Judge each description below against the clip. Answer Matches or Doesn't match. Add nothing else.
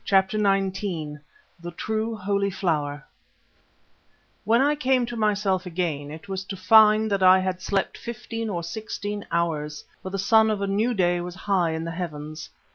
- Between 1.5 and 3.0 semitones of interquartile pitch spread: Doesn't match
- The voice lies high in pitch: Matches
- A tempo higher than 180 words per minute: Doesn't match